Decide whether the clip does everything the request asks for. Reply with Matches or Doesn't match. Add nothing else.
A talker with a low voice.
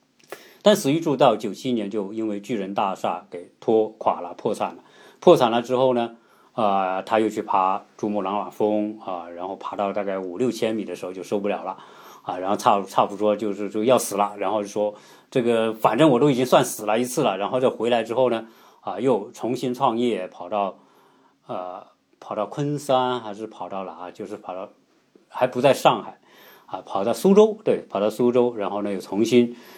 Matches